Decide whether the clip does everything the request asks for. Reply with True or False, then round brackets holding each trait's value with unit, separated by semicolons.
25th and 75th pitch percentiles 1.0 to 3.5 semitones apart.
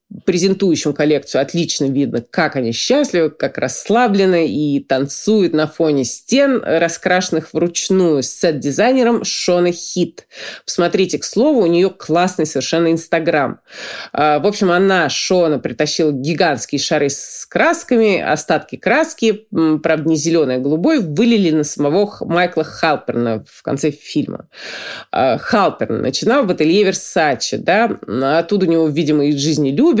False (4.2 semitones)